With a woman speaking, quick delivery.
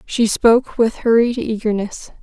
No: female; slow, 135 wpm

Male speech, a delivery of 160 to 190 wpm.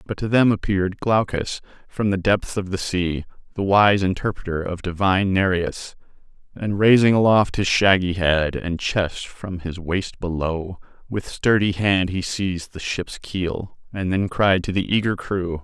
Yes: male; average, 170 wpm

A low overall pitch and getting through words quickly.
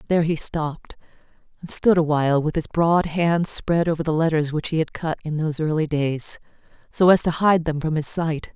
No: medium, 160 Hz; fast, 215 wpm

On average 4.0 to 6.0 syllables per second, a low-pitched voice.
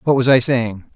Yes: 5.1 syllables/s; low, 125 Hz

